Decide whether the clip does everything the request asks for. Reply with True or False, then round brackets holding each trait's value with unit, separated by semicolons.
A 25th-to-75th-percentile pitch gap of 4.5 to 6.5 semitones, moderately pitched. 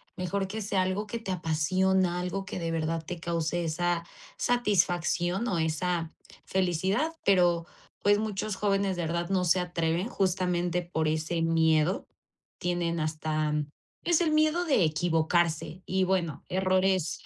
False (2.6 semitones; 180 Hz)